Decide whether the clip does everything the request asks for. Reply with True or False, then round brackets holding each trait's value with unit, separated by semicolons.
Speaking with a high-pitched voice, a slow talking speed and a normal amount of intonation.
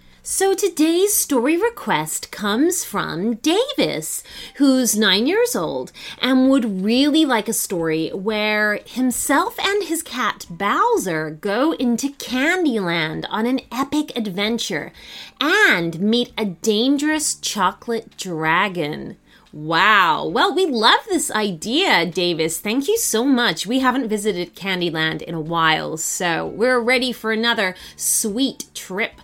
False (235 Hz; 125 wpm; 6.1 semitones)